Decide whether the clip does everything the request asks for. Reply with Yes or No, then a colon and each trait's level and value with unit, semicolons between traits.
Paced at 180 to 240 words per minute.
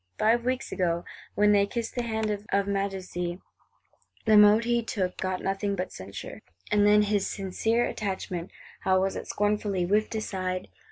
No: average, 160 wpm